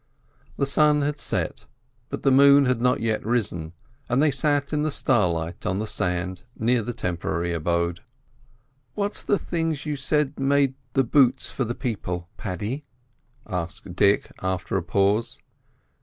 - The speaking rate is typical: Yes, average, 155 wpm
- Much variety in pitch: Yes, wide, 7.7 semitones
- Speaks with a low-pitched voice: Yes, low, 120 Hz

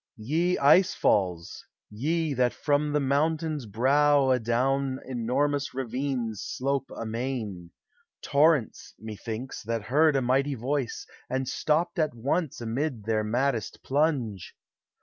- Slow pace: Yes, slow, 120 wpm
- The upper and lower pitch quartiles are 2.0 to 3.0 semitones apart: No, average, 4.1 semitones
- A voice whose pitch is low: Yes, low, 130 Hz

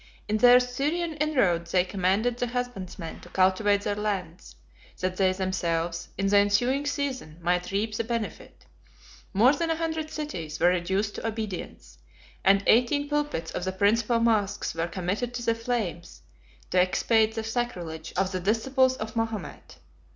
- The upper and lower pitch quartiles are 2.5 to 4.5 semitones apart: No, average, 5.0 semitones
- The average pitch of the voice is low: No, high, 210 Hz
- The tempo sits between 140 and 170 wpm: Yes, average, 160 wpm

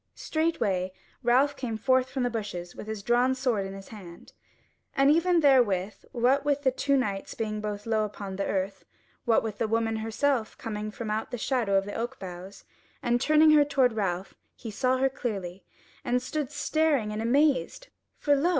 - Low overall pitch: No, high, 230 Hz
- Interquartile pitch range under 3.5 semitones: No, average, 4.7 semitones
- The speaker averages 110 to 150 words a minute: No, average, 185 wpm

